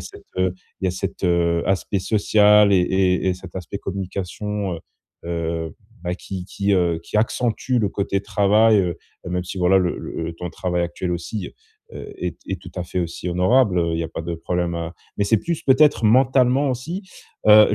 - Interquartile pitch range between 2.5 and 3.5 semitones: Yes, average, 3.2 semitones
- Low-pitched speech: Yes, very low, 95 Hz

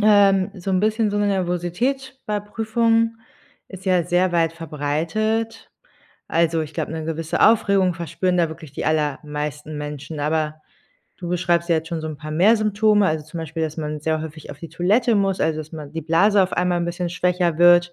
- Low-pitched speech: No, medium, 175 Hz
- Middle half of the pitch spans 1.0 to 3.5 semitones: No, average, 4.1 semitones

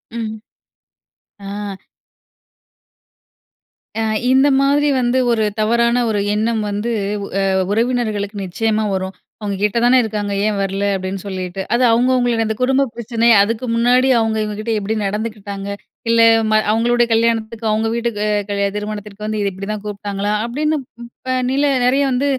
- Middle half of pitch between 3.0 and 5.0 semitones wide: No, narrow, 2.6 semitones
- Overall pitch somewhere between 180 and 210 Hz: No, high, 220 Hz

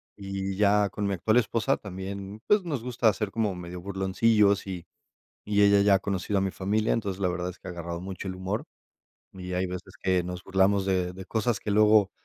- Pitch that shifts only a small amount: Yes, narrow, 2.2 semitones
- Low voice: Yes, low, 100 Hz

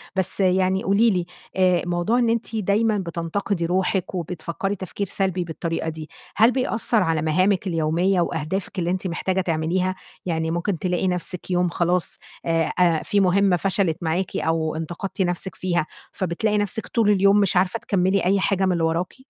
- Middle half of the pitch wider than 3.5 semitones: No, narrow, 2.6 semitones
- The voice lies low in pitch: No, medium, 185 Hz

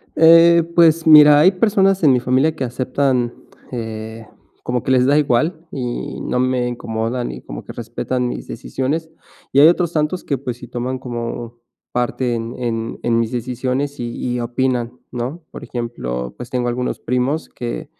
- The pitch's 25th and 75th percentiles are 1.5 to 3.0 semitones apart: No, average, 3.7 semitones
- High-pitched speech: No, low, 125 Hz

